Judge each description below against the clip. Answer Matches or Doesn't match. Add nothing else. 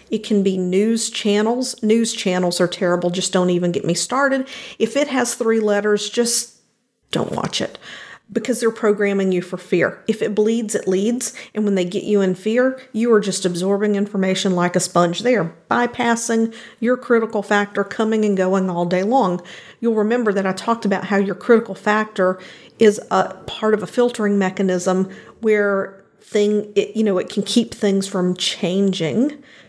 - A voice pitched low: Doesn't match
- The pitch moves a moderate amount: Matches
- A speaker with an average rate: Matches